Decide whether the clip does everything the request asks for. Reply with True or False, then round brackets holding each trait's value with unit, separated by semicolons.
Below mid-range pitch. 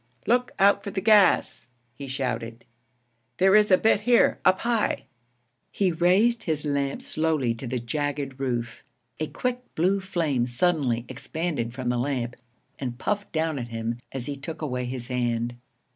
False (145 Hz)